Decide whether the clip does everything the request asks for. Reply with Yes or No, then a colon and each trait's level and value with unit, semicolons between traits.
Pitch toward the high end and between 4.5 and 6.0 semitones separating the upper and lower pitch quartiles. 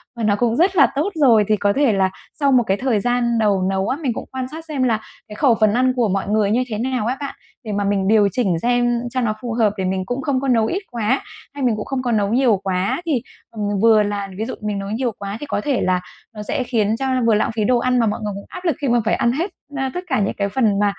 No: high, 230 Hz; average, 3.8 semitones